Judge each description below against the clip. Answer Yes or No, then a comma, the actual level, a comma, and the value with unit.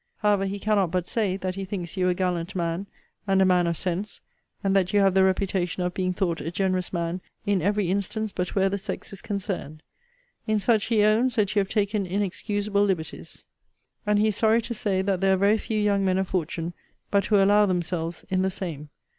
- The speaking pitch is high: Yes, high, 195 Hz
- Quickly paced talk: Yes, fast, 220 wpm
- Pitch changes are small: Yes, narrow, 2.2 semitones